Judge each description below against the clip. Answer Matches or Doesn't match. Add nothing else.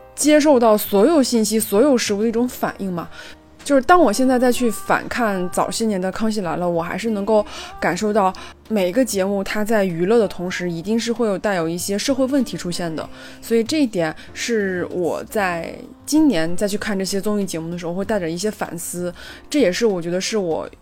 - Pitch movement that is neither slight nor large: Matches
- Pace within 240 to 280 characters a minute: Doesn't match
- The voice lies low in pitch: Doesn't match